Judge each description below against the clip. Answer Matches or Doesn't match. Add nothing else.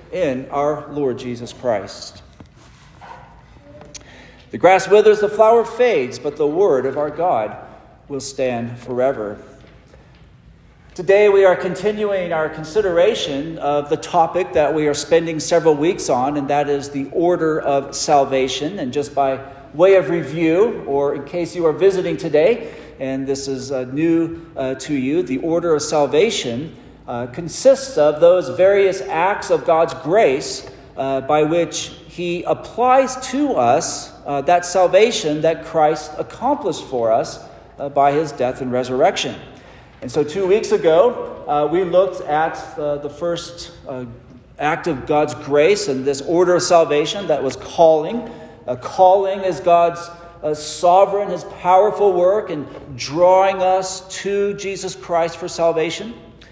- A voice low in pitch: Doesn't match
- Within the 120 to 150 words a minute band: Matches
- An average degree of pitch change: Matches